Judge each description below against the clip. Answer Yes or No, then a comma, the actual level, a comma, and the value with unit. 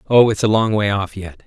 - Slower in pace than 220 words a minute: No, fast, 285 wpm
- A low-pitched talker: Yes, low, 105 Hz